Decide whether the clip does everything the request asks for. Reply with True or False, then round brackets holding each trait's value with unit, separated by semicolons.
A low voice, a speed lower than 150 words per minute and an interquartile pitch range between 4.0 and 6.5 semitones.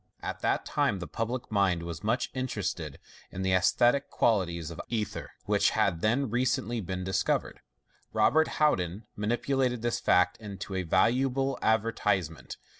True (105 Hz; 140 wpm; 4.9 semitones)